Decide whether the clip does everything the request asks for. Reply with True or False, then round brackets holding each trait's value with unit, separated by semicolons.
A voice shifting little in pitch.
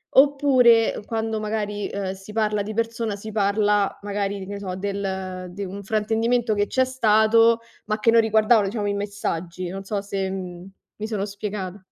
True (2.0 semitones)